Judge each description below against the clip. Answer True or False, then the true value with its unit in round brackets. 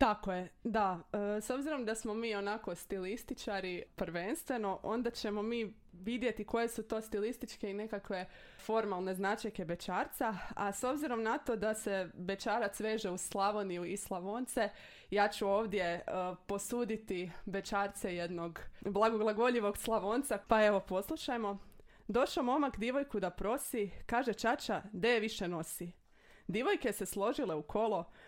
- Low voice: False (210 Hz)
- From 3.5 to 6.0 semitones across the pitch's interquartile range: False (3.0 semitones)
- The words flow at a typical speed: True (140 wpm)